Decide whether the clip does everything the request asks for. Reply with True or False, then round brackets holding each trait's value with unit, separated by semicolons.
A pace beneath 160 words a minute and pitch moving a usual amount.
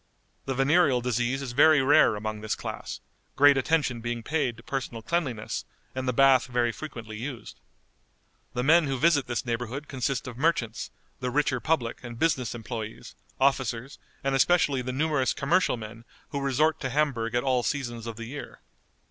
False (170 wpm; 3.2 semitones)